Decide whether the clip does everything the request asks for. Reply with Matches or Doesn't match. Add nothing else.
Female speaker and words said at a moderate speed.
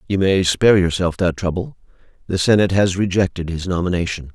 Doesn't match